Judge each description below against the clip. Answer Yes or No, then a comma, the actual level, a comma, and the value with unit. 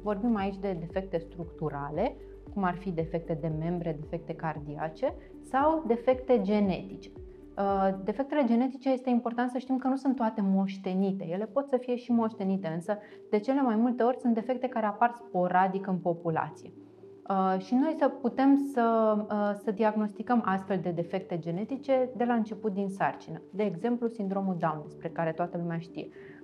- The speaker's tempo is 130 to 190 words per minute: Yes, average, 160 wpm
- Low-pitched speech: No, high, 210 Hz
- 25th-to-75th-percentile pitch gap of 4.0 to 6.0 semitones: Yes, wide, 5.5 semitones